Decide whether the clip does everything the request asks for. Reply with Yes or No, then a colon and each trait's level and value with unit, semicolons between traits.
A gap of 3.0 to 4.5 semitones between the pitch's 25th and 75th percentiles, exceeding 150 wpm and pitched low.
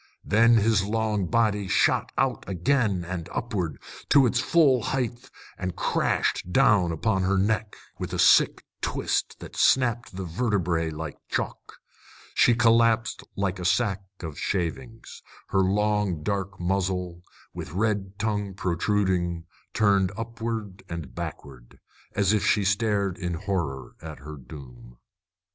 No: average, 4.0 semitones; slow, 135 wpm; low, 100 Hz